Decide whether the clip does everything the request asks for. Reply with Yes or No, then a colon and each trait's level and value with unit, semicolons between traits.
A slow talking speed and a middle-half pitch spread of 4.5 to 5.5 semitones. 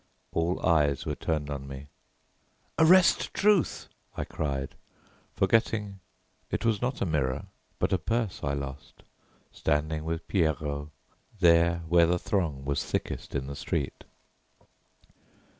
Yes: slow, 125 wpm; average, 5.2 semitones